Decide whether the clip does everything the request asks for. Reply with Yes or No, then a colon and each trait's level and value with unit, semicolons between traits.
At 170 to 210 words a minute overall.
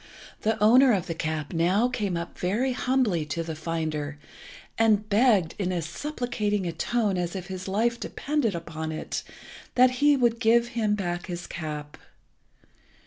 No: average, 160 wpm